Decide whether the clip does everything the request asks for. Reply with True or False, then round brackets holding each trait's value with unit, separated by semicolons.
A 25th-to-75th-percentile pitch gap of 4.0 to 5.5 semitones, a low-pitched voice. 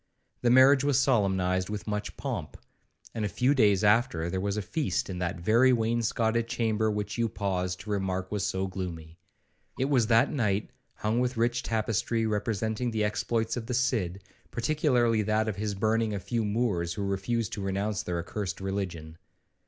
False (3.4 semitones; 105 Hz)